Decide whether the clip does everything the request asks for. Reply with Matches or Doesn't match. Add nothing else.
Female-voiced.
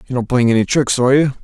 Doesn't match